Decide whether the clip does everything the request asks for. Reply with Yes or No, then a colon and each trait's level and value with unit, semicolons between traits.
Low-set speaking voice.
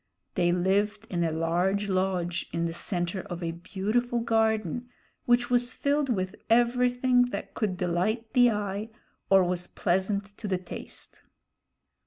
No: high, 200 Hz